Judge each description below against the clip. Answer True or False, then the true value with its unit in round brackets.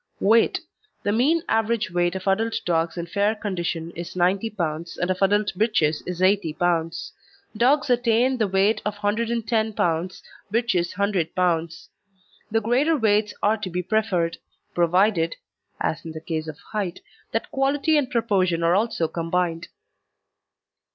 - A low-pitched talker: False (195 Hz)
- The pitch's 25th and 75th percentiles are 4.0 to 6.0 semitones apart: True (4.6 semitones)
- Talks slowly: False (145 wpm)